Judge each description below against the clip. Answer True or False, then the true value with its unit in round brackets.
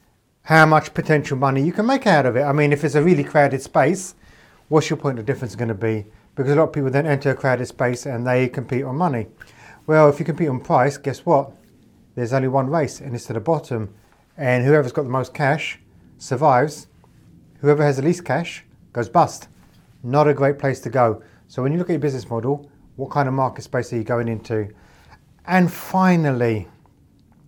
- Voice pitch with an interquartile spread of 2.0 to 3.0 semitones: False (3.6 semitones)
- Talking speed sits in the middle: False (215 wpm)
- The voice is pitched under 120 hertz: False (140 Hz)